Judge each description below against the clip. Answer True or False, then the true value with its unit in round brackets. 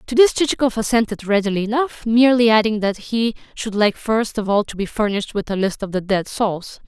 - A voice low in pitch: False (215 Hz)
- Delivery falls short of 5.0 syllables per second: False (5.7 syllables/s)